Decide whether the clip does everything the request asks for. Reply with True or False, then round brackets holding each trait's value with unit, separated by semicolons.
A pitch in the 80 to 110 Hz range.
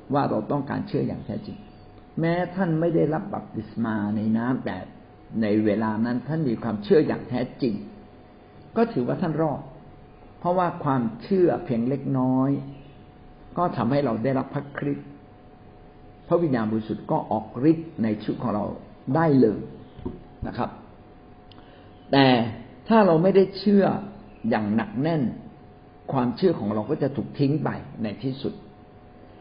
False (135 Hz)